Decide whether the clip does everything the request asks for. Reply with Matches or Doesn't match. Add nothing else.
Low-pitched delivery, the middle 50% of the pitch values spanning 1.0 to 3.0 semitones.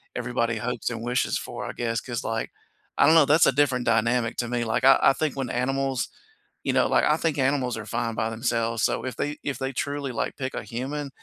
Matches